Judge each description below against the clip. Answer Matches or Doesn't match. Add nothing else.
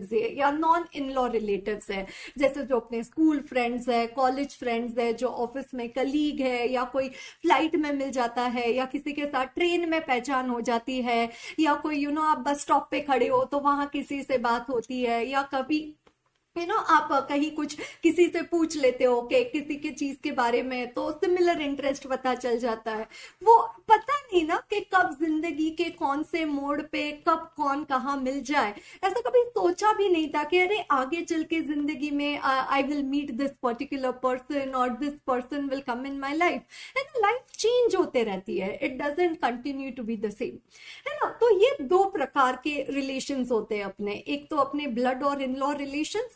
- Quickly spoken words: Matches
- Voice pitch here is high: Matches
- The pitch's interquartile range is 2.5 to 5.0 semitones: Matches